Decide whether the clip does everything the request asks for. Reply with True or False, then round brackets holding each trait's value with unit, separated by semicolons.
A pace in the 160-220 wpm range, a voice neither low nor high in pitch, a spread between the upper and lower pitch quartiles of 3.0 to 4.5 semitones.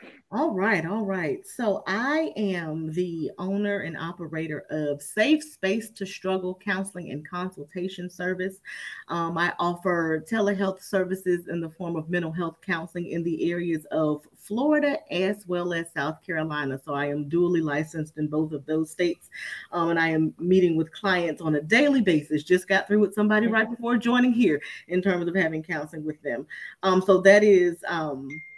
True (175 wpm; 180 Hz; 3.8 semitones)